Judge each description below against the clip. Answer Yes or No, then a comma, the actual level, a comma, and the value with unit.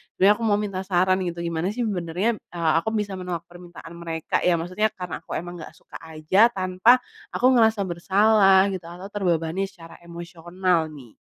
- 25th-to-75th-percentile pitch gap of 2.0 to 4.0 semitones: Yes, average, 2.8 semitones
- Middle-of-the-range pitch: Yes, medium, 180 Hz